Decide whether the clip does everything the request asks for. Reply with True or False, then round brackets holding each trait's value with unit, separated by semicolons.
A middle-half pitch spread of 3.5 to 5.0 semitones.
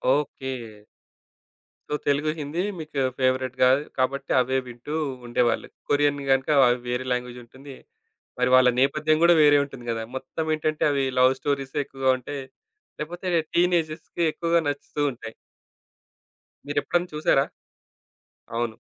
False (3.0 semitones)